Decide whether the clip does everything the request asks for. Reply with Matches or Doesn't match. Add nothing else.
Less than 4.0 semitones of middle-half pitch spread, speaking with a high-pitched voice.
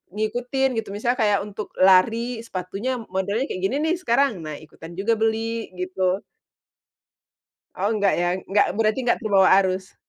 Matches